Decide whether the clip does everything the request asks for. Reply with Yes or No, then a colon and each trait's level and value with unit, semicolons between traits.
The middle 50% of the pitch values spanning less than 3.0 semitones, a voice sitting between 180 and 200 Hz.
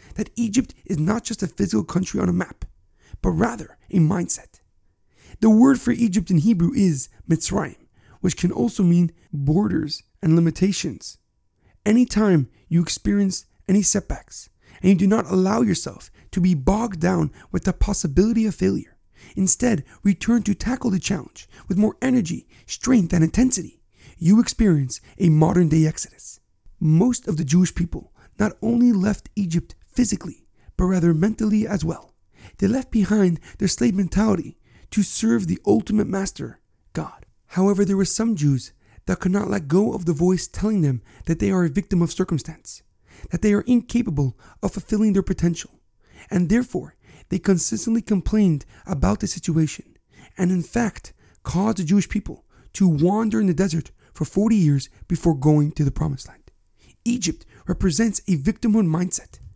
No: average, 4.6 semitones; medium, 185 Hz